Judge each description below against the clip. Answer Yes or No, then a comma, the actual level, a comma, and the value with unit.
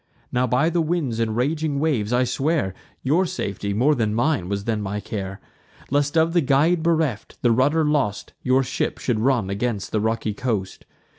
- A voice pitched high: No, low, 125 Hz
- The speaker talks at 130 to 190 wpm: Yes, average, 180 wpm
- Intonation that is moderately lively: No, wide, 6.0 semitones